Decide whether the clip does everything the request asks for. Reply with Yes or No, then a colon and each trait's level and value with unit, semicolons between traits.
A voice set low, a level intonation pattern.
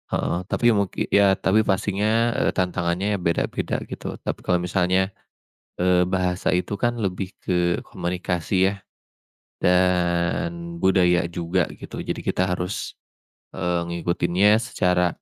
Yes: very low, 90 Hz; narrow, 2.1 semitones